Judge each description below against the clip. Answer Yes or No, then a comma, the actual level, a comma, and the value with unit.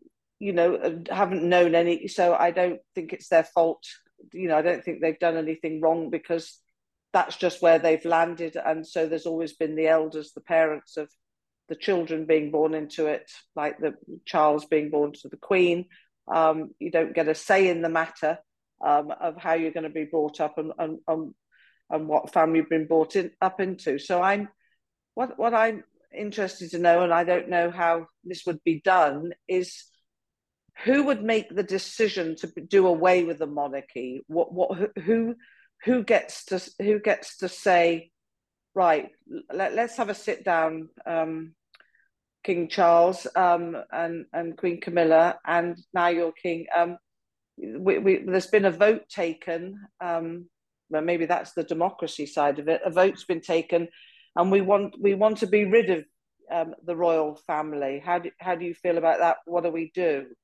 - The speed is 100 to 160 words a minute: No, average, 185 wpm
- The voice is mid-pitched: Yes, medium, 170 Hz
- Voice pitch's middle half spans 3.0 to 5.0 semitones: No, narrow, 2.6 semitones